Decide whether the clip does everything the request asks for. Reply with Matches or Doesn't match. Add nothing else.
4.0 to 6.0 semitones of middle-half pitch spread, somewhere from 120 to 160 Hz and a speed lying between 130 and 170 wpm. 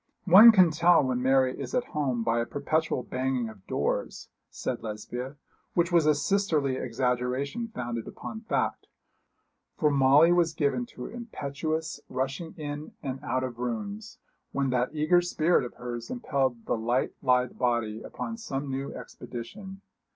Matches